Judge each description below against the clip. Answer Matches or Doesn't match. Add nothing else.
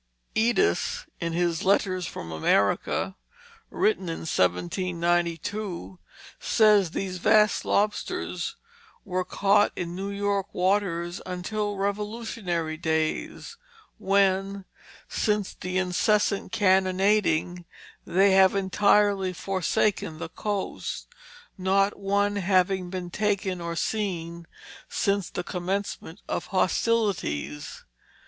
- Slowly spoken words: Matches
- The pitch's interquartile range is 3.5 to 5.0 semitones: Doesn't match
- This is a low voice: Doesn't match